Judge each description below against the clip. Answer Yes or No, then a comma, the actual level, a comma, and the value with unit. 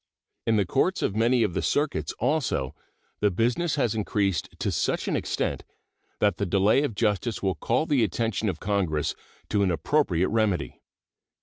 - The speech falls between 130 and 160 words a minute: No, average, 170 wpm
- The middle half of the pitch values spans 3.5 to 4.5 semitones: Yes, average, 4.0 semitones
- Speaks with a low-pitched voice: Yes, low, 105 Hz